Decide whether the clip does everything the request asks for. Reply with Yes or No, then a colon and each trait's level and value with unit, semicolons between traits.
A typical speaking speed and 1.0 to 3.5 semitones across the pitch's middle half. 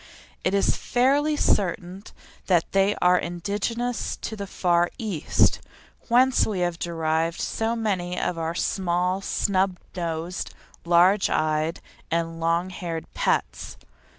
No: slow, 125 wpm; average, 3.2 semitones